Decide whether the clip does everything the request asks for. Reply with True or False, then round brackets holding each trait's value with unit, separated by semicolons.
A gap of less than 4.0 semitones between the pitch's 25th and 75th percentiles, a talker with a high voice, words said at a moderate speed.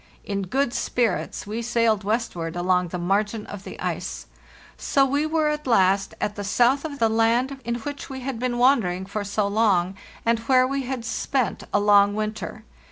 False (4.3 semitones; 225 Hz; 185 wpm)